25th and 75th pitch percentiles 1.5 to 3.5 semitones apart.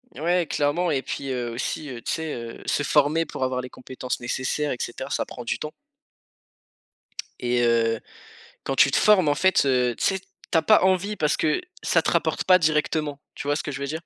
No: average, 4.1 semitones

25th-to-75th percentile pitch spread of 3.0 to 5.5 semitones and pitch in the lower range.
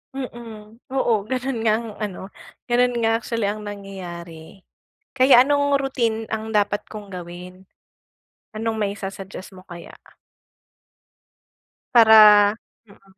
No: average, 3.3 semitones; high, 215 Hz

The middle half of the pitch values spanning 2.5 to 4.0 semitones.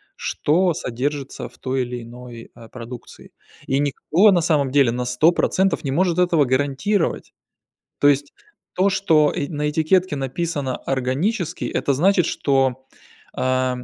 No: average, 4.6 semitones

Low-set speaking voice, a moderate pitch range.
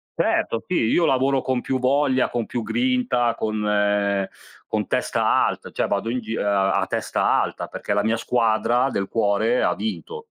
Yes: low, 115 Hz; average, 4.2 semitones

